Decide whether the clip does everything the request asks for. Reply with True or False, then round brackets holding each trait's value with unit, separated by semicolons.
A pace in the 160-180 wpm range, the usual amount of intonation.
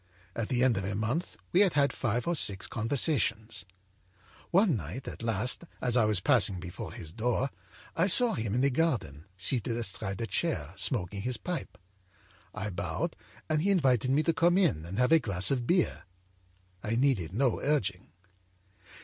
False (175 wpm; 6.8 semitones)